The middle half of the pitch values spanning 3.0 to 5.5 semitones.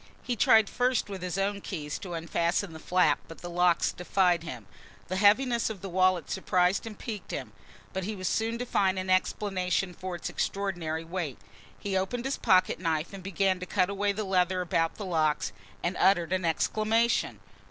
No: narrow, 2.6 semitones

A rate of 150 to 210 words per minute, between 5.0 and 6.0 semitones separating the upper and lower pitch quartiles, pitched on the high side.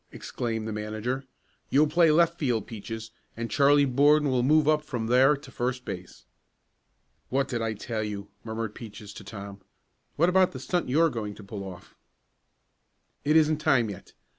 No: average, 175 wpm; average, 5.3 semitones; low, 125 Hz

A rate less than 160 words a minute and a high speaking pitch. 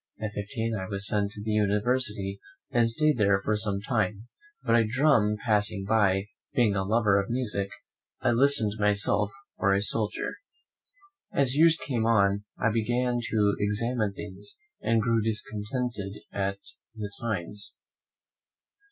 No: average, 145 wpm; low, 105 Hz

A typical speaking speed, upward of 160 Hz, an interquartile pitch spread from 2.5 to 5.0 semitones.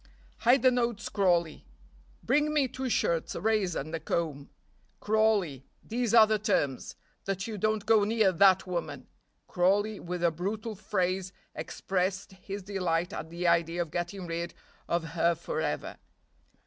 Yes: average, 155 wpm; high, 190 Hz; average, 4.1 semitones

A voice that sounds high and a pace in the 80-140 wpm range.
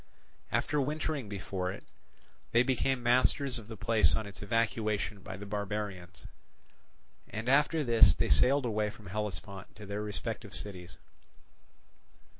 No: low, 105 Hz; slow, 135 wpm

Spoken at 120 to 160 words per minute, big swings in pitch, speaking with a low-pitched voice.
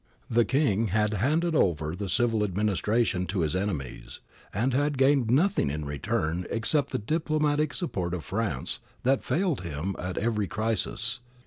Yes: average, 150 wpm; wide, 6.7 semitones; low, 110 Hz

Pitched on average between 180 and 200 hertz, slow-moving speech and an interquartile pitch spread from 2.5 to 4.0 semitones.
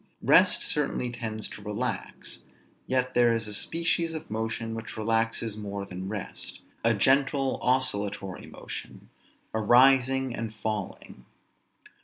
No: low, 115 Hz; slow, 125 wpm; average, 3.3 semitones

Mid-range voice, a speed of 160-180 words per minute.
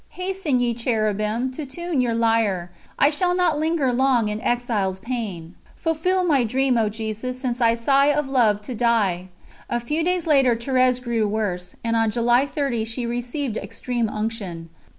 No: high, 240 Hz; average, 170 wpm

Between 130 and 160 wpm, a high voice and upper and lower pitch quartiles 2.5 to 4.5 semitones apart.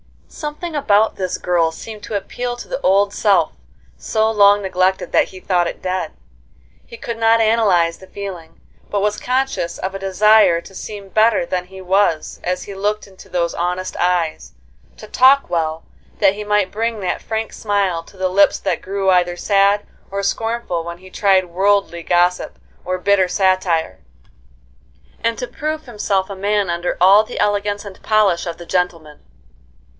No: average, 170 wpm; high, 195 Hz; average, 2.8 semitones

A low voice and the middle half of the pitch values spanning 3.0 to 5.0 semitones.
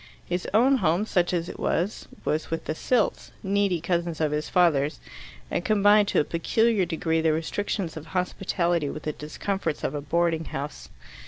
No: medium, 170 Hz; average, 3.8 semitones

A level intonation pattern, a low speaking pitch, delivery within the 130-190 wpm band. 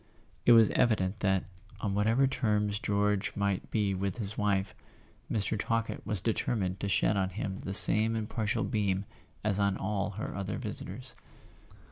Yes: narrow, 2.1 semitones; low, 105 Hz; average, 155 wpm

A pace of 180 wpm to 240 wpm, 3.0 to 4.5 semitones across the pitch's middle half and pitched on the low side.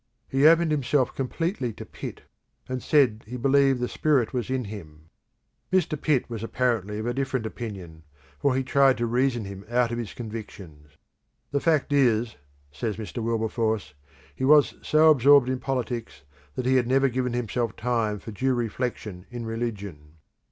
No: average, 165 wpm; average, 3.5 semitones; low, 120 Hz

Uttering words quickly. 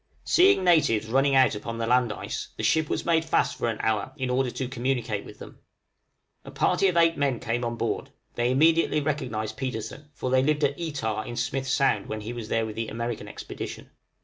Yes: fast, 210 wpm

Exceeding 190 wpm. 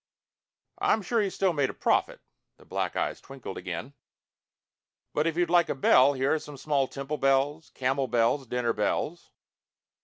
No: average, 160 wpm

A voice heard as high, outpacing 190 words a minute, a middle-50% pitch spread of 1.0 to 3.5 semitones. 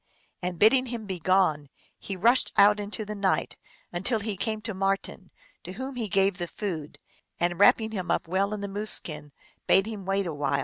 Yes: high, 195 Hz; fast, 205 wpm; average, 3.0 semitones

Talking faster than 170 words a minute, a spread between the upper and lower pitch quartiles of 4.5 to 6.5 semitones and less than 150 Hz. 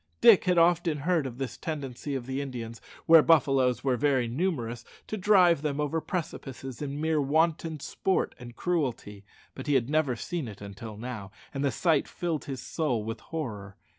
Yes: average, 180 wpm; average, 4.8 semitones; medium, 140 Hz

